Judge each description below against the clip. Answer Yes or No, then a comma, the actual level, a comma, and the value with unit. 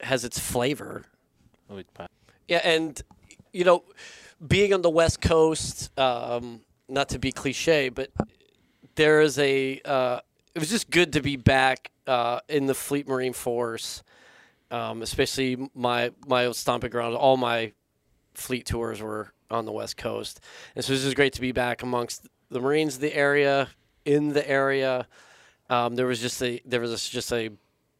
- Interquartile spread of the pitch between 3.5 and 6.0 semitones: No, average, 3.1 semitones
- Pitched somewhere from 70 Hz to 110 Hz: No, low, 130 Hz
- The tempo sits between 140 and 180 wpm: Yes, average, 165 wpm